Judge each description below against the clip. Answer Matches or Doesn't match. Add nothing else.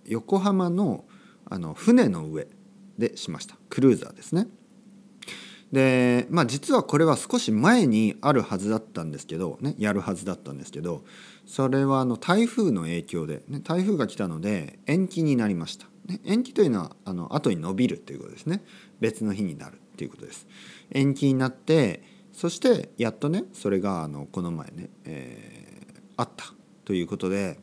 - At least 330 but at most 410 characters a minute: Matches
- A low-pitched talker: Doesn't match